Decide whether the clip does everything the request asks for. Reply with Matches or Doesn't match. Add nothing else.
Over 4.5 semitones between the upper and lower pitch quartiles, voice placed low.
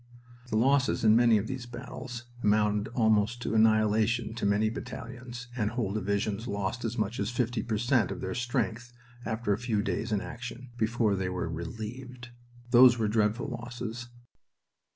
Doesn't match